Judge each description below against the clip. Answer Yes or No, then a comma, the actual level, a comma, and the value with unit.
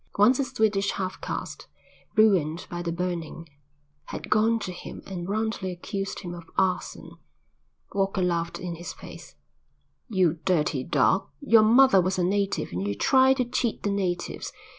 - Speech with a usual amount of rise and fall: Yes, average, 3.7 semitones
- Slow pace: No, average, 160 wpm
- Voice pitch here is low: No, high, 190 Hz